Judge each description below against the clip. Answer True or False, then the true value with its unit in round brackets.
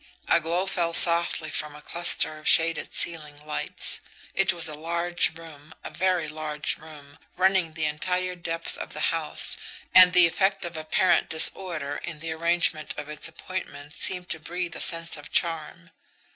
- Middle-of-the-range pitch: True (165 Hz)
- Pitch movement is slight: True (2.2 semitones)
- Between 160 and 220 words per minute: True (170 wpm)